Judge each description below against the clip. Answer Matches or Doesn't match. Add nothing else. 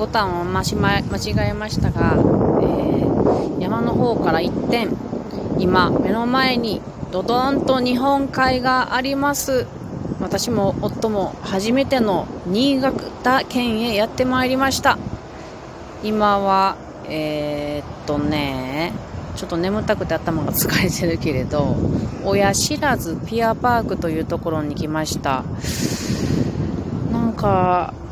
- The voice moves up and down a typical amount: Doesn't match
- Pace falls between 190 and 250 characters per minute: Matches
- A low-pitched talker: Doesn't match